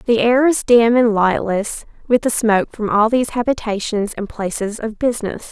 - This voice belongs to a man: No, female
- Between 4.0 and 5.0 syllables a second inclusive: Yes, 4.9 syllables/s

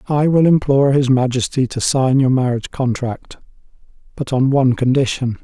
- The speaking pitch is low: Yes, low, 130 Hz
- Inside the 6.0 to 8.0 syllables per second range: No, 5.4 syllables/s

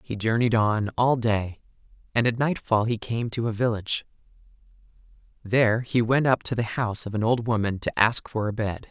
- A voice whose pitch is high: No, low, 115 Hz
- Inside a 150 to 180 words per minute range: No, average, 195 wpm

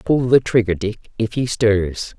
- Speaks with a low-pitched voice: Yes, low, 110 Hz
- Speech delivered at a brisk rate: No, average, 190 wpm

